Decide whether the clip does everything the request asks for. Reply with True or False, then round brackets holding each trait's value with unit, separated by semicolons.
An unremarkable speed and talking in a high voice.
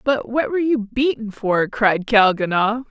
True (165 wpm; 230 Hz)